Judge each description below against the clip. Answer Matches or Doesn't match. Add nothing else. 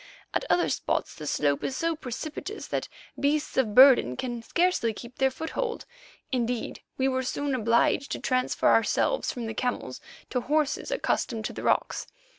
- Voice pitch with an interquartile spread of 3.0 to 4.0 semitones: Doesn't match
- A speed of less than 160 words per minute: Doesn't match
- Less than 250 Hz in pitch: Doesn't match